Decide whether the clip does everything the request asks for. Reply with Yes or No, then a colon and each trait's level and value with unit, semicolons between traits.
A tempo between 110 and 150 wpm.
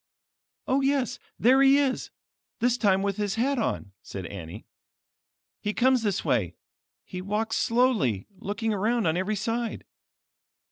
Yes: average, 140 wpm